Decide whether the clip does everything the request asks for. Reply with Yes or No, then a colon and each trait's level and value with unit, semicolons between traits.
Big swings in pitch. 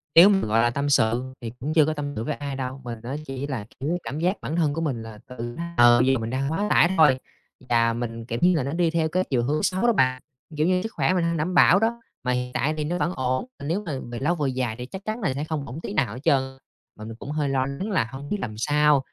No: average, 4.8 semitones